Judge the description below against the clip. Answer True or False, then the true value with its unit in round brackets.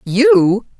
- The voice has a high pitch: True (260 Hz)